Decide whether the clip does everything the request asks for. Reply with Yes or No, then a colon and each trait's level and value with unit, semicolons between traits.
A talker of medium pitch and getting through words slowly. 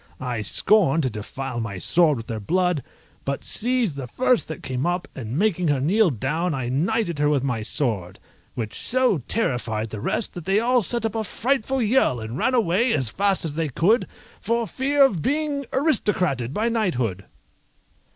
No: medium, 165 Hz; average, 180 wpm